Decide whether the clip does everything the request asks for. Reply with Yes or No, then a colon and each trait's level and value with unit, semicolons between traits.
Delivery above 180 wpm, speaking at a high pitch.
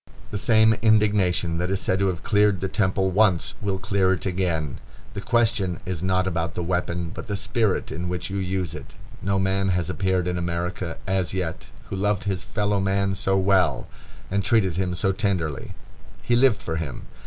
No: average, 190 wpm; very low, 95 Hz